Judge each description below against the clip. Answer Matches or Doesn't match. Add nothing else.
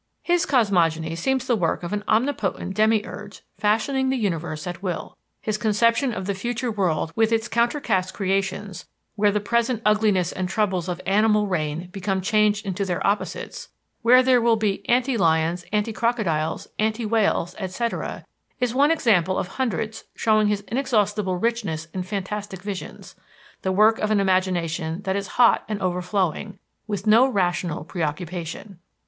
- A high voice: Matches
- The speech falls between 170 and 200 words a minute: Doesn't match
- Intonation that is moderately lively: Matches